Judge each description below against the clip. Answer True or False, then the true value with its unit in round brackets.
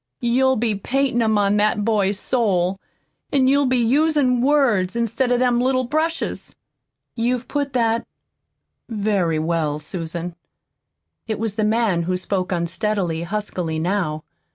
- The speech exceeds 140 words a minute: False (135 wpm)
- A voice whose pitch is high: True (215 Hz)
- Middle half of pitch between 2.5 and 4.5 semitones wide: False (5.4 semitones)